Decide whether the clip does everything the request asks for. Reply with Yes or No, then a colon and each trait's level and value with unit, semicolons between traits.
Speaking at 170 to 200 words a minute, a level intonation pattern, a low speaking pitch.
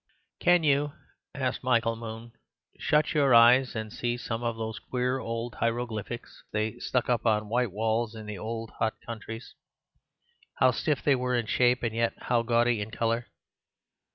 No: average, 160 wpm; narrow, 2.0 semitones; low, 115 Hz